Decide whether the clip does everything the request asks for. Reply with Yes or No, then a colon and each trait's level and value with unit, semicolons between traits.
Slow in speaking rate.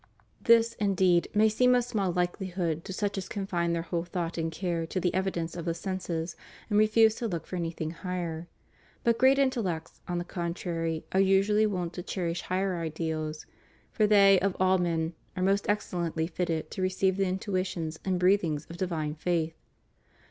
No: average, 180 wpm